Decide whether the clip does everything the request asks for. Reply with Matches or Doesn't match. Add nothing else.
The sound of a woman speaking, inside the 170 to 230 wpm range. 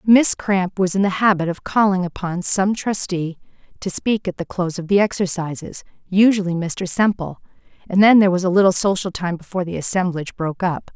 Matches